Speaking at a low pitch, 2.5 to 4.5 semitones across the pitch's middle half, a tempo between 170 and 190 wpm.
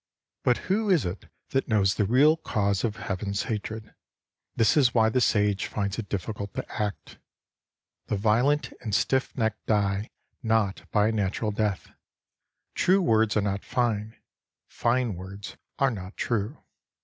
No: low, 110 Hz; average, 2.9 semitones; average, 150 wpm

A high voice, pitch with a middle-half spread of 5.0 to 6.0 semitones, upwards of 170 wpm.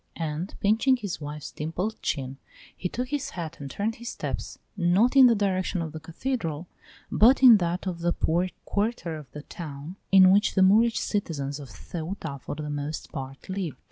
No: medium, 175 Hz; average, 5.3 semitones; average, 185 wpm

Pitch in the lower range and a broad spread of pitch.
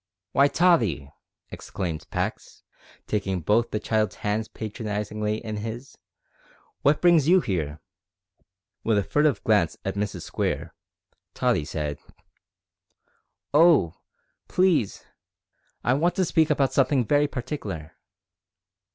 Yes: low, 110 Hz; wide, 6.7 semitones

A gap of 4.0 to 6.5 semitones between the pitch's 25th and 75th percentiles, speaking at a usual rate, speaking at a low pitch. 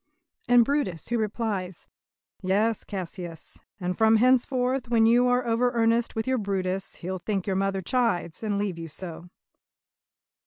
No: average, 4.3 semitones; average, 150 wpm; high, 210 Hz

